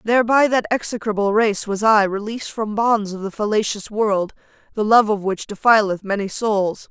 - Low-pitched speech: No, high, 210 Hz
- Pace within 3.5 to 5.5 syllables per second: Yes, 5.0 syllables/s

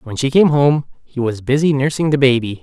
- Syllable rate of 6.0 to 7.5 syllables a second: No, 5.5 syllables/s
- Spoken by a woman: No, male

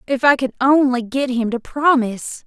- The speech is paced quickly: No, average, 195 wpm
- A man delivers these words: No, female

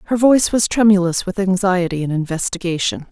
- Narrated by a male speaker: No, female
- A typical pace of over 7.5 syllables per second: No, 5.9 syllables/s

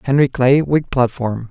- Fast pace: No, average, 160 wpm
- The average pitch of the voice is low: Yes, low, 130 Hz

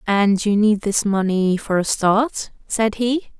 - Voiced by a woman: Yes, female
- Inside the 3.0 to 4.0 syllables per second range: Yes, 3.6 syllables/s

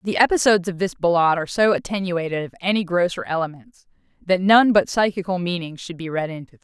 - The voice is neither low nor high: Yes, medium, 180 Hz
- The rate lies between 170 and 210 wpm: Yes, average, 200 wpm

